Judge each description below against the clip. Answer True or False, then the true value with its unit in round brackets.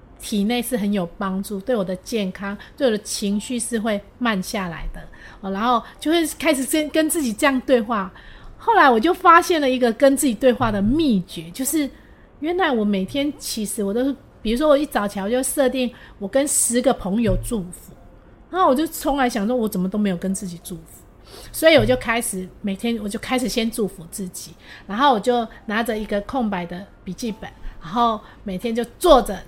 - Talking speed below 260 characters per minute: False (295 characters per minute)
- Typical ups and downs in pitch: True (4.8 semitones)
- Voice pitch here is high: True (235 Hz)